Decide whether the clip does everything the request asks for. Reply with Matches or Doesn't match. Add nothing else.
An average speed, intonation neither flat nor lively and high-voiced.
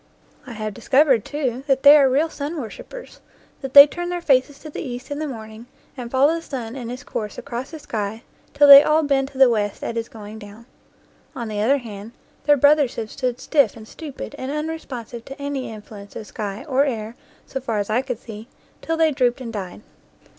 Doesn't match